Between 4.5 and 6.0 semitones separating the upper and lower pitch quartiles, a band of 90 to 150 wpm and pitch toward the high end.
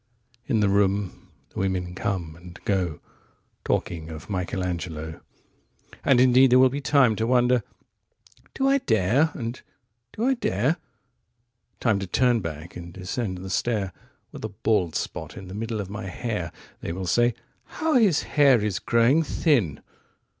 No: wide, 5.5 semitones; average, 140 wpm; low, 105 Hz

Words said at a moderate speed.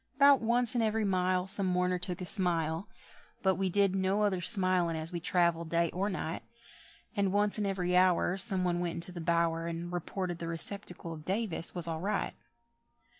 Yes: average, 190 wpm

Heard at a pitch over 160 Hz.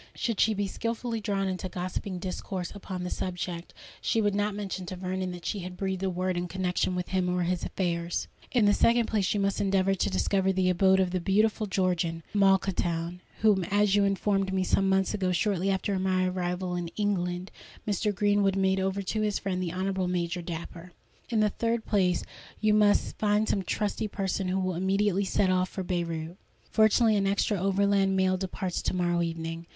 Yes: high, 190 Hz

